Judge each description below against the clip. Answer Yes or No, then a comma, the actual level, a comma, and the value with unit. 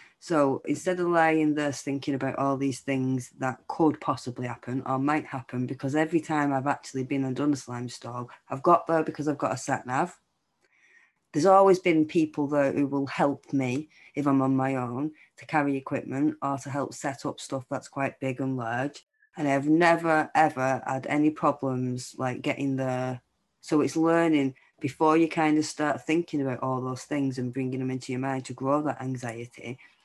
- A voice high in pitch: No, medium, 140 Hz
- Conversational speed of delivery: Yes, average, 190 wpm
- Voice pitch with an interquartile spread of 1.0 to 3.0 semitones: Yes, narrow, 2.6 semitones